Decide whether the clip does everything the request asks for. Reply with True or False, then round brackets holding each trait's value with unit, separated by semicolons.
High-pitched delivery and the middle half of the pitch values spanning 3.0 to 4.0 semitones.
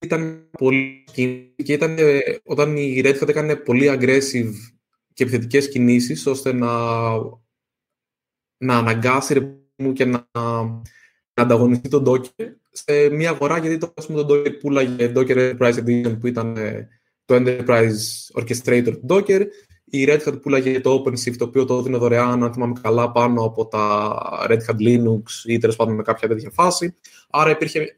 False (125 Hz; 3.3 semitones)